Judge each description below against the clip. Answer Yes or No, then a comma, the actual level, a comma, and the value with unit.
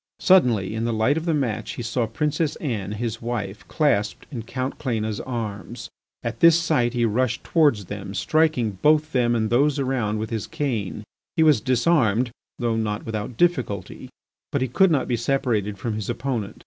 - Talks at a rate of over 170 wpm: Yes, average, 180 wpm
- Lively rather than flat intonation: No, average, 4.6 semitones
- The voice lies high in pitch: No, low, 120 Hz